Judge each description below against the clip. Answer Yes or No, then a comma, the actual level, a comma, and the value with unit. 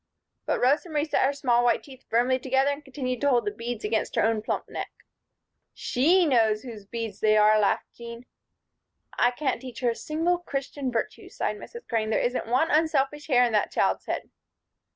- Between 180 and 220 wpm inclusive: Yes, average, 195 wpm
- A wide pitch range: No, average, 3.7 semitones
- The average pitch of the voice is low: No, very high, 250 Hz